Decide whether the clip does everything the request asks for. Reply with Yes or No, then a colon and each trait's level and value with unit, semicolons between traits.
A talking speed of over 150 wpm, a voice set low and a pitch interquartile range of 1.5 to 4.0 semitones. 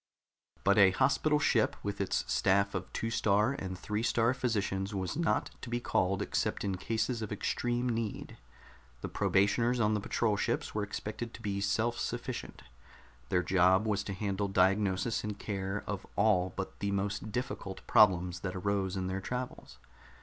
Yes: average, 170 wpm; low, 100 Hz; average, 2.8 semitones